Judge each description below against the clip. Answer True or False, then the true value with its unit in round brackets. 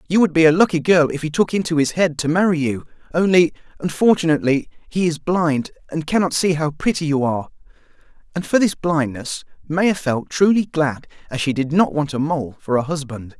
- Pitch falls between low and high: True (155 Hz)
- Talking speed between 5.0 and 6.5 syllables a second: True (5.5 syllables/s)